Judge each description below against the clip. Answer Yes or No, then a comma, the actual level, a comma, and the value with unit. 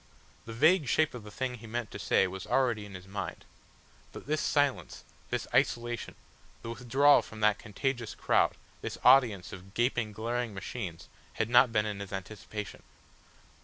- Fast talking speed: No, average, 165 wpm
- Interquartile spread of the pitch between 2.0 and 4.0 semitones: Yes, average, 3.4 semitones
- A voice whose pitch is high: No, low, 115 Hz